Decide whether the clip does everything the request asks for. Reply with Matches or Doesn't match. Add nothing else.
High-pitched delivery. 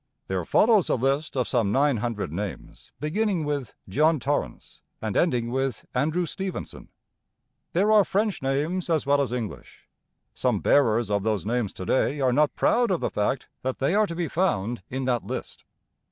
Doesn't match